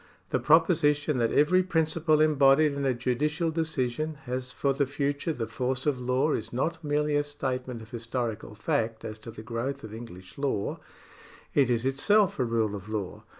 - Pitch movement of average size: Yes, average, 4.4 semitones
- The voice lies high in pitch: No, low, 135 Hz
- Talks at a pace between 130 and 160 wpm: No, average, 180 wpm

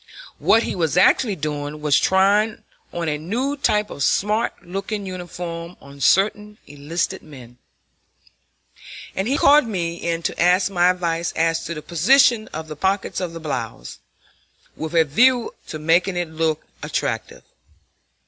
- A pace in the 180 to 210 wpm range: No, average, 150 wpm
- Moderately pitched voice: Yes, medium, 175 Hz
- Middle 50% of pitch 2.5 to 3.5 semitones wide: No, average, 4.3 semitones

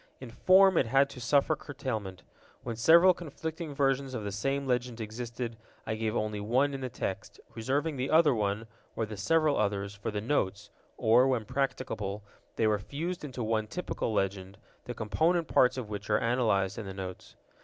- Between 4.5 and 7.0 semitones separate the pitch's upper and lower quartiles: Yes, average, 4.8 semitones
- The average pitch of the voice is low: Yes, low, 120 Hz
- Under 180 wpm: No, average, 185 wpm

